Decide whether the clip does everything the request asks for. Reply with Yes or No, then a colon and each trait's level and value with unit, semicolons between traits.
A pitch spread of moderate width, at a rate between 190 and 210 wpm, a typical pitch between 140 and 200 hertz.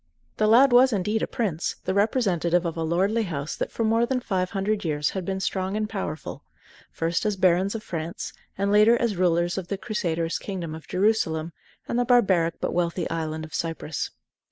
Yes: average, 4.4 semitones; average, 195 wpm; high, 190 Hz